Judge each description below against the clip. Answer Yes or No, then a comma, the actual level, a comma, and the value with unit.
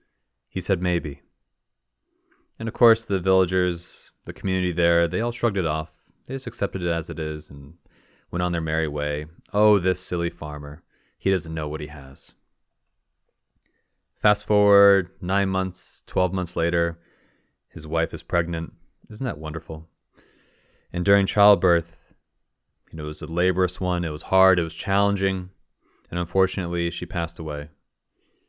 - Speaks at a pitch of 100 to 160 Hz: No, very low, 85 Hz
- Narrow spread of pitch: No, average, 3.0 semitones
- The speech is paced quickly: No, average, 155 wpm